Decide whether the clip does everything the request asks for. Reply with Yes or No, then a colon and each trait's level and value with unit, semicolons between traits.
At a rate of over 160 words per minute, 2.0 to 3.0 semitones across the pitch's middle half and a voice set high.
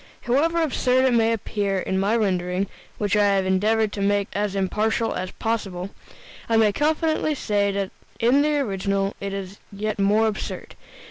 Yes: average, 170 wpm; narrow, 2.6 semitones; high, 205 Hz